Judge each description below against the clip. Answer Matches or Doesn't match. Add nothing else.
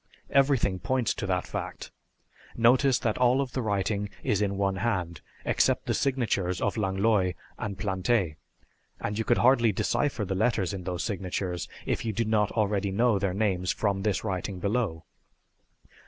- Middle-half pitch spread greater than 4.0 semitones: Doesn't match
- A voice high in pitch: Doesn't match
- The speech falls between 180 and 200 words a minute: Doesn't match